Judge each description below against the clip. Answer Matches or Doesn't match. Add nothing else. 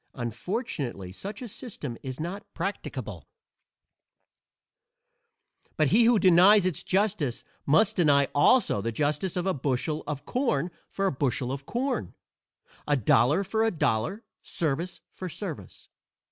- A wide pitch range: Matches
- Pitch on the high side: Doesn't match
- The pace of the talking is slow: Matches